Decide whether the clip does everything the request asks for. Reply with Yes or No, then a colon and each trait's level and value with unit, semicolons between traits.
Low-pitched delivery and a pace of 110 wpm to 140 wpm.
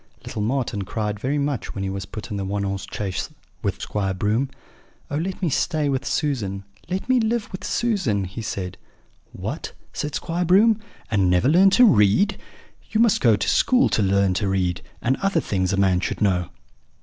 No: low, 110 Hz; average, 195 wpm